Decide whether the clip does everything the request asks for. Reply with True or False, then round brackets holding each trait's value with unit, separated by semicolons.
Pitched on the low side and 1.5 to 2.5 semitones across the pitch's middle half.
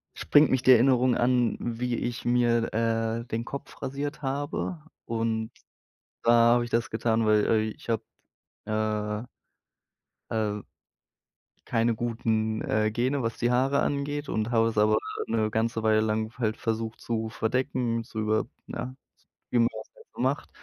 True (115 Hz; 1.9 semitones)